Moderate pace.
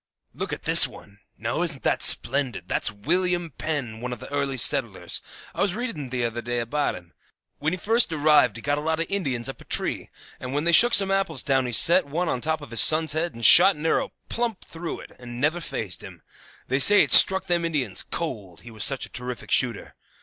No: fast, 225 wpm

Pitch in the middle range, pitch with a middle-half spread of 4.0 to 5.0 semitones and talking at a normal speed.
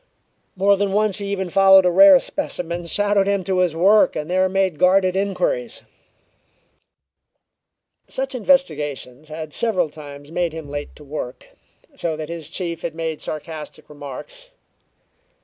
Yes: medium, 180 Hz; average, 4.4 semitones; average, 145 wpm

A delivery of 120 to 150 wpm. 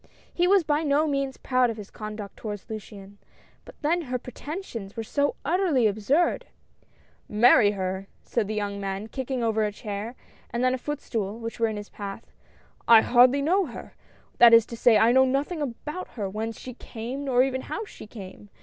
No: fast, 205 wpm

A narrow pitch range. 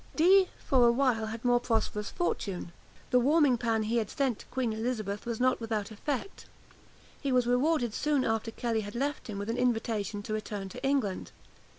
No: average, 3.1 semitones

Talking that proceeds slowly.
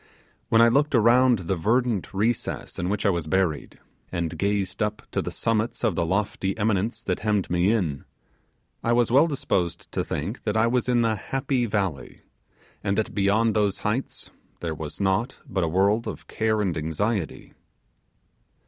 No: average, 175 wpm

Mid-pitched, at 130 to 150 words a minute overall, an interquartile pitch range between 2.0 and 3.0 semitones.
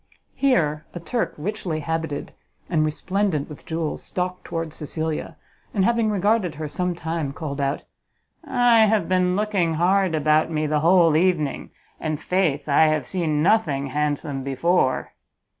No: medium, 165 Hz; average, 145 wpm; average, 3.5 semitones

